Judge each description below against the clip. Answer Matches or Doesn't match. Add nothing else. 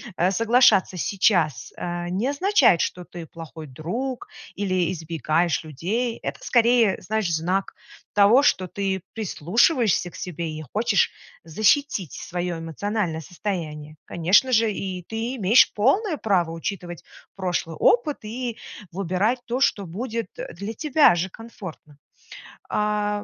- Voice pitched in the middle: Doesn't match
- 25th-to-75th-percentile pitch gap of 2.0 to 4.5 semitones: Doesn't match